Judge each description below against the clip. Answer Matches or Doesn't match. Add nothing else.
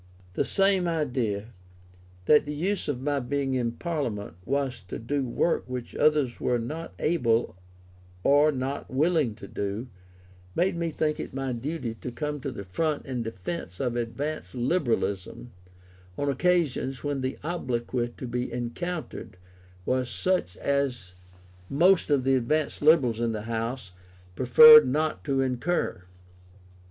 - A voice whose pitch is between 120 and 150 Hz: Matches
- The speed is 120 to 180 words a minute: Matches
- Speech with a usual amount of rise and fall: Matches